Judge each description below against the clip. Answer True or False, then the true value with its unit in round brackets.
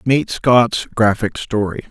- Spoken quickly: False (125 wpm)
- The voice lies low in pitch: True (115 Hz)